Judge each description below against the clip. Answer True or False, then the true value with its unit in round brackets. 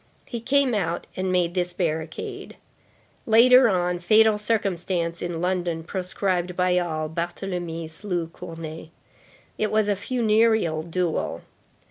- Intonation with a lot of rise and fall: False (3.8 semitones)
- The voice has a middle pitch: True (180 Hz)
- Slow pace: True (120 wpm)